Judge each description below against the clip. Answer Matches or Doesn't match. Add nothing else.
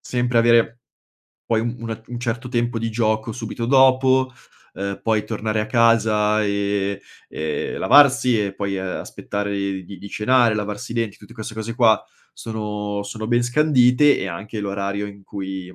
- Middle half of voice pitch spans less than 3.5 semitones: Matches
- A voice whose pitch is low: Matches